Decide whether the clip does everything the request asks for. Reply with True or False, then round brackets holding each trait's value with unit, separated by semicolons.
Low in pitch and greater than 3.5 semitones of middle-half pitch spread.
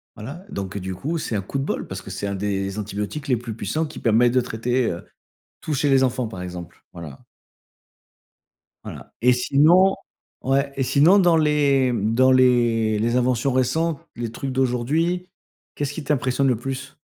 True (125 Hz; 4.1 semitones)